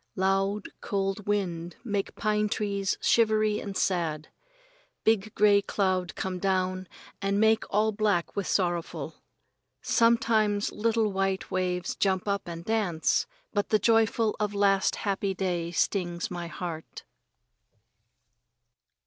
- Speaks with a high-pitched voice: Yes, high, 195 Hz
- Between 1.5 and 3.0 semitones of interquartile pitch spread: Yes, narrow, 2.4 semitones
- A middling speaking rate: No, slow, 120 wpm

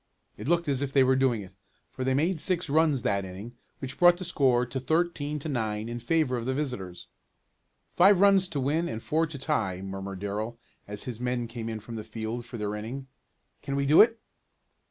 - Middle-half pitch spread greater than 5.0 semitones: Yes, wide, 5.5 semitones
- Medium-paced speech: No, fast, 215 wpm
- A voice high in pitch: No, low, 130 Hz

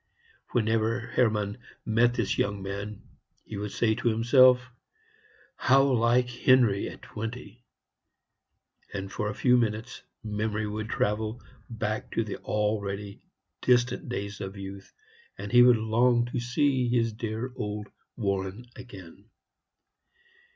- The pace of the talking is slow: Yes, slow, 125 wpm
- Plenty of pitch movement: No, average, 2.8 semitones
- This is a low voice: Yes, low, 110 Hz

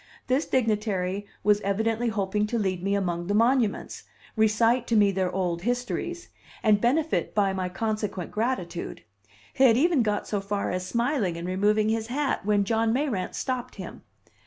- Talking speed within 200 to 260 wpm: No, average, 165 wpm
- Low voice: No, high, 210 Hz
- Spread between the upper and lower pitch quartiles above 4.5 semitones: No, average, 3.6 semitones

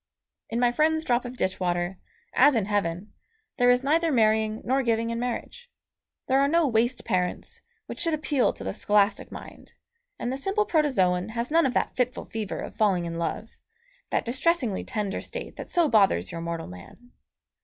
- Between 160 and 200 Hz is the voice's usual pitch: No, high, 235 Hz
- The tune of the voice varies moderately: No, wide, 5.7 semitones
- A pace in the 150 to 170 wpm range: No, average, 185 wpm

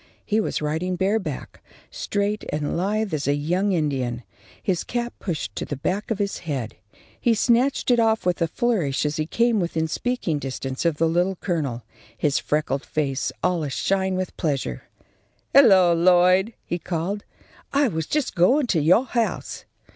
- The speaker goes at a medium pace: Yes, average, 165 wpm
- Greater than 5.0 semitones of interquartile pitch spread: Yes, wide, 5.6 semitones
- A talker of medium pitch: Yes, medium, 175 Hz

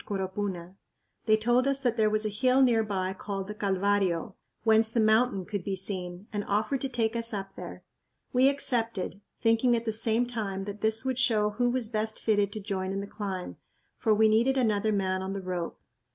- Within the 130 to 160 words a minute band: No, fast, 205 wpm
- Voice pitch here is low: No, high, 215 Hz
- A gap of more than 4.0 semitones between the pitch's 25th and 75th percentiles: No, average, 2.9 semitones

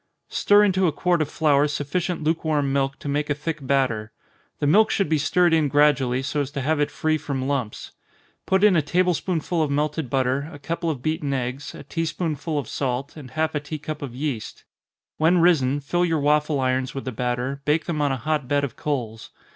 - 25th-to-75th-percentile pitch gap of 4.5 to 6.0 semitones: No, average, 2.8 semitones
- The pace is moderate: No, fast, 220 wpm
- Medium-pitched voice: Yes, medium, 145 Hz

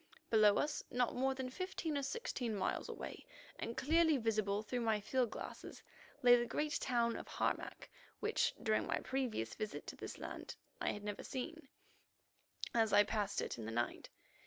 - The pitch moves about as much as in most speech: Yes, average, 4.2 semitones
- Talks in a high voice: Yes, high, 240 Hz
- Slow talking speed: No, average, 175 wpm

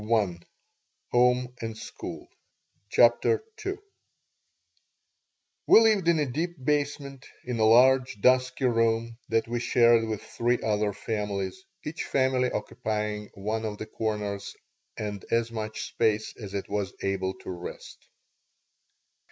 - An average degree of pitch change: Yes, average, 3.4 semitones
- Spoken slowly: Yes, slow, 125 wpm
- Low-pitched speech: Yes, low, 115 Hz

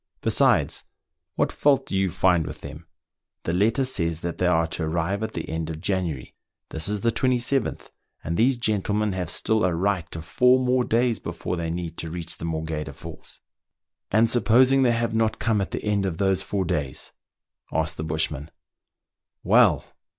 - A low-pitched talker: Yes, very low, 95 Hz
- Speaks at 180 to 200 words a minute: Yes, average, 190 wpm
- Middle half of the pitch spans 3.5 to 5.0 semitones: No, wide, 5.5 semitones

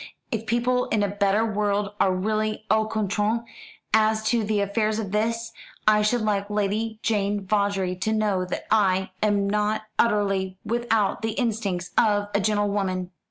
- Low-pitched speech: No, high, 210 Hz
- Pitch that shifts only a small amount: Yes, narrow, 1.6 semitones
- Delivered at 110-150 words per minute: No, average, 160 wpm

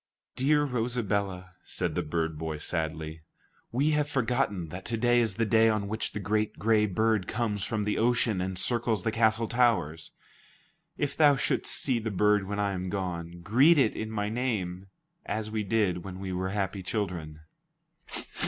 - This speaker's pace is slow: No, average, 175 wpm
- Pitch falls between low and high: No, low, 105 Hz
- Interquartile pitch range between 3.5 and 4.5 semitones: Yes, average, 4.0 semitones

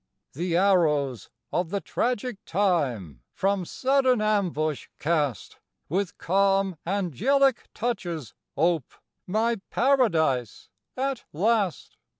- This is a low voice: No, high, 190 Hz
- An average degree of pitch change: No, wide, 5.9 semitones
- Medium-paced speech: No, slow, 95 wpm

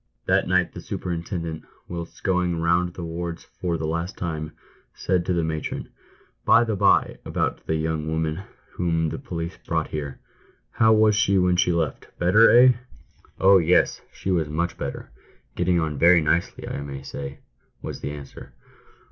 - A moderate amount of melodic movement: No, narrow, 2.3 semitones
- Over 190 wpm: No, average, 180 wpm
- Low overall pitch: Yes, very low, 85 Hz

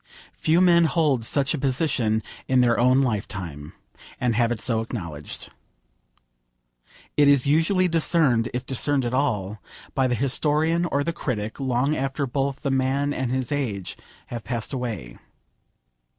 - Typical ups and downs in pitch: Yes, average, 3.7 semitones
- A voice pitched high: No, low, 130 Hz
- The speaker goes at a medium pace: Yes, average, 150 wpm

